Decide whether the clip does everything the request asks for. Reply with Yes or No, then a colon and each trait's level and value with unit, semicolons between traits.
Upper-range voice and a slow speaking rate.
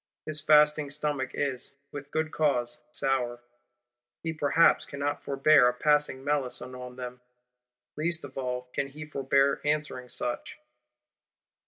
No: medium, 140 Hz; slow, 130 wpm